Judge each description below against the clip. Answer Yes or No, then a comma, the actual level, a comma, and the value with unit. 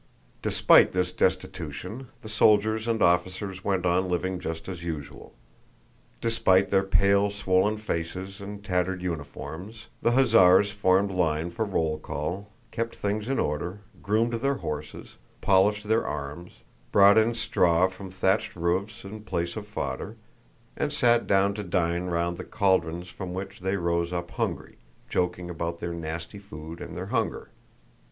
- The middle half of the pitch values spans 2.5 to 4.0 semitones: Yes, average, 3.1 semitones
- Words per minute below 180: Yes, average, 150 wpm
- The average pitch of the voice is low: Yes, very low, 95 Hz